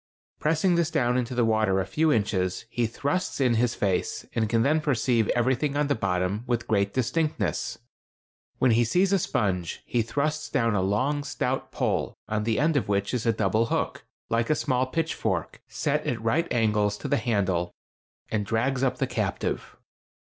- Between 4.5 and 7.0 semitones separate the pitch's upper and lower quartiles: Yes, average, 5.0 semitones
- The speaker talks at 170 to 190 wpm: Yes, average, 185 wpm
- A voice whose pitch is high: No, low, 120 Hz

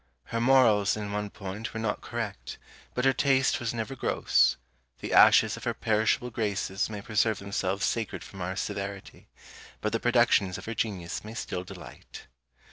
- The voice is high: No, low, 105 Hz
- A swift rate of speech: No, average, 170 wpm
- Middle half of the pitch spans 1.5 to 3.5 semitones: Yes, average, 2.7 semitones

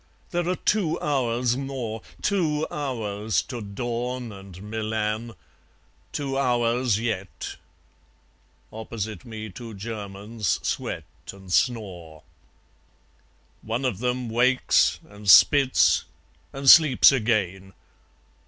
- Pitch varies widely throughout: No, average, 3.6 semitones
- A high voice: No, low, 115 Hz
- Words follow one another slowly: Yes, slow, 95 wpm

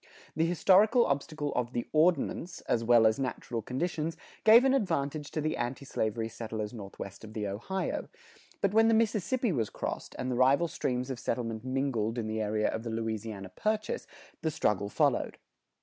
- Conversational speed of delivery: Yes, average, 175 wpm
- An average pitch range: No, wide, 7.0 semitones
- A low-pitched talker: Yes, low, 130 Hz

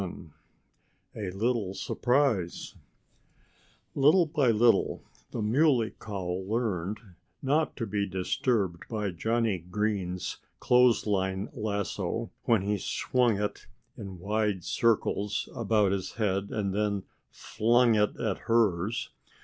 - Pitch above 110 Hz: No, low, 105 Hz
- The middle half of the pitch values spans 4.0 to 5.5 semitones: No, average, 3.3 semitones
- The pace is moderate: No, slow, 110 wpm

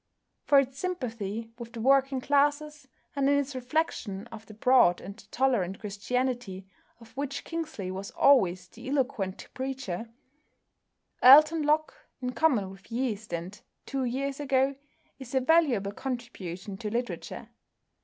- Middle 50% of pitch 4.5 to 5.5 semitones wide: Yes, average, 5.1 semitones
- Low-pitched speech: No, very high, 250 Hz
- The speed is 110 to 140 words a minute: Yes, slow, 135 wpm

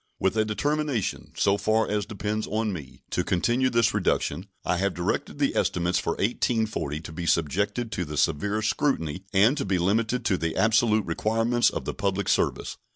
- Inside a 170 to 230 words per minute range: Yes, average, 180 wpm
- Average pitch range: Yes, average, 4.1 semitones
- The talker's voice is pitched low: Yes, low, 105 Hz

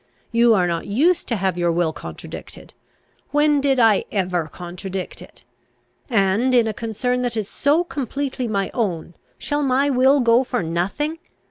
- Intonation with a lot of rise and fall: Yes, wide, 6.0 semitones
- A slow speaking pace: No, average, 160 wpm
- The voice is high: Yes, high, 230 Hz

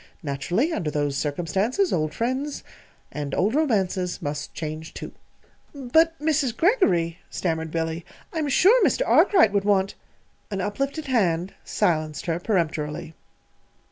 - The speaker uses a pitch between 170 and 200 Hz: Yes, high, 190 Hz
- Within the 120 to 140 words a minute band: Yes, slow, 135 wpm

